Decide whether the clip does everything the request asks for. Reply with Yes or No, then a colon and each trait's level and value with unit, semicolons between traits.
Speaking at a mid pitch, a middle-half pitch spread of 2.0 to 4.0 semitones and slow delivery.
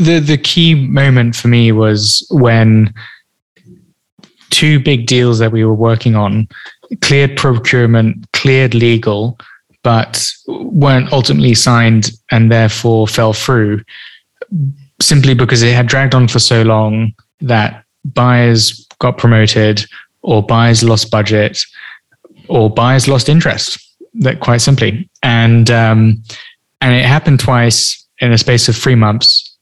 No: low, 120 Hz; average, 3.1 semitones; slow, 130 wpm